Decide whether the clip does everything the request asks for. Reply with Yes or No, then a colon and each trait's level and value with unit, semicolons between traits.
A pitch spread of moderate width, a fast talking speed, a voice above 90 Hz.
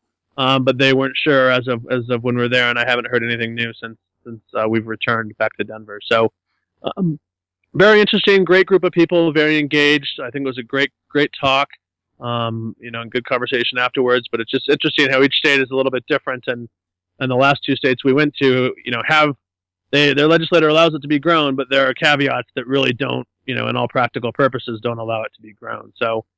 Yes: average, 3.7 semitones; fast, 235 wpm; low, 130 Hz